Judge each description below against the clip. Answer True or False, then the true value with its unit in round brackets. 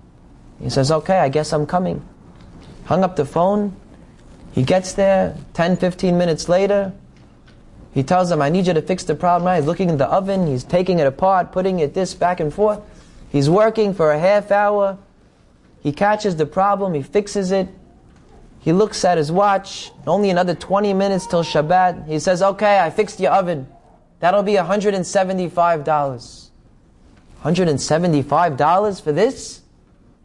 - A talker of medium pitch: True (180 Hz)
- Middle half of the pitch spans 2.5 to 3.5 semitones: False (4.0 semitones)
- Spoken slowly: False (160 wpm)